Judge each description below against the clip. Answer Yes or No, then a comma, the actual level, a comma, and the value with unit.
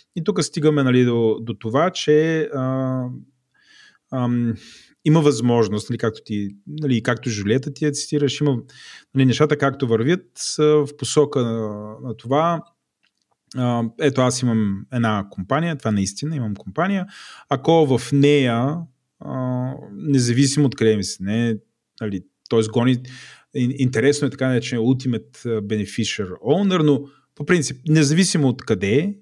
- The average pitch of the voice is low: Yes, low, 130 Hz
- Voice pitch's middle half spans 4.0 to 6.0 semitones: Yes, average, 4.3 semitones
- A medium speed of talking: Yes, average, 145 wpm